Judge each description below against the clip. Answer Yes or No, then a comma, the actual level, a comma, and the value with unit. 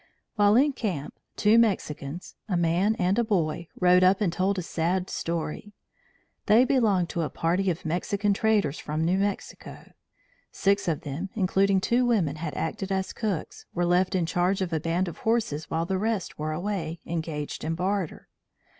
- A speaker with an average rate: Yes, average, 175 wpm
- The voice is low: No, medium, 185 Hz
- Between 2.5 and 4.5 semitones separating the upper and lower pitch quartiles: Yes, average, 3.6 semitones